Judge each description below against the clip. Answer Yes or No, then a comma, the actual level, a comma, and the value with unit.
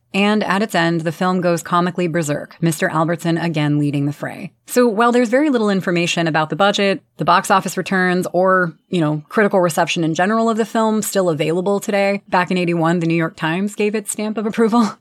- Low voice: No, medium, 185 Hz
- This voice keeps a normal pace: No, fast, 210 wpm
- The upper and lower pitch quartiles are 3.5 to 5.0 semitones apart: Yes, average, 3.9 semitones